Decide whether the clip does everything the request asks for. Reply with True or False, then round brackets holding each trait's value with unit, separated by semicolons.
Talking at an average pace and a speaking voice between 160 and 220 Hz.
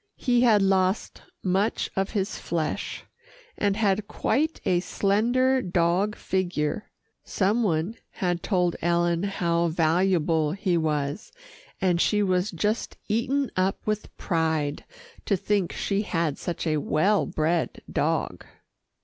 False (130 wpm; 185 Hz)